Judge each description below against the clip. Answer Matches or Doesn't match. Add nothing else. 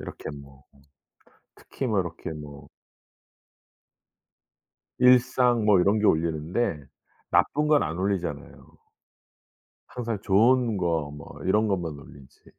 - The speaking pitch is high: Doesn't match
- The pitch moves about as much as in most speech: Doesn't match